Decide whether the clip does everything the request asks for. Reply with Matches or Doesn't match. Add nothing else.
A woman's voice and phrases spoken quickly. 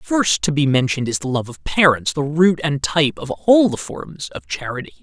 Doesn't match